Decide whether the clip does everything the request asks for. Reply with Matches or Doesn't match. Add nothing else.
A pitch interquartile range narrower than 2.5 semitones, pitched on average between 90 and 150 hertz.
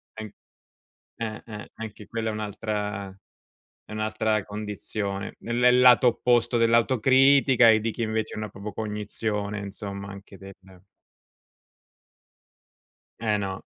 Matches